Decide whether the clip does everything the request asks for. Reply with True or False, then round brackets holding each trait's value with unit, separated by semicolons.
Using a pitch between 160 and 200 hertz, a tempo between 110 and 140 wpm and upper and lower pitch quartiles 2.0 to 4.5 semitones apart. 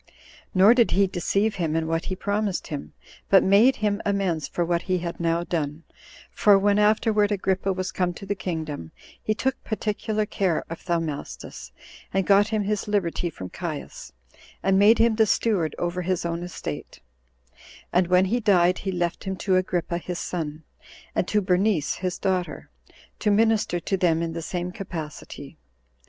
False (185 Hz; 175 wpm; 3.2 semitones)